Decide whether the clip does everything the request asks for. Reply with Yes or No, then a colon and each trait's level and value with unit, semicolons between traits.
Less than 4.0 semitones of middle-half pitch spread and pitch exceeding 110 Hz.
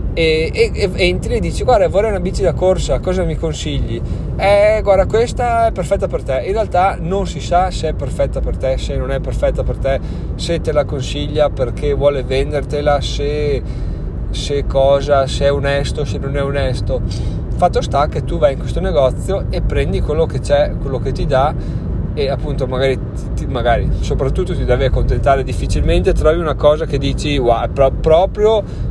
Yes: average, 3.5 semitones; medium, 140 Hz